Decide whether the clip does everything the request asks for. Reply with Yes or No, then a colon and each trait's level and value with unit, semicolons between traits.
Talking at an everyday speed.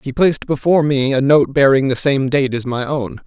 No: fast, 240 wpm